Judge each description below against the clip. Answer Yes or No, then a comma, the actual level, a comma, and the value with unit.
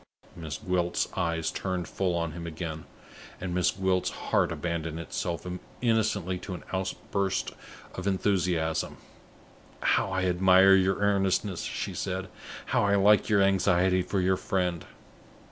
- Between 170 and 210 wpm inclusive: No, slow, 135 wpm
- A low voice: Yes, very low, 95 Hz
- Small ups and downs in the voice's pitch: Yes, narrow, 1.9 semitones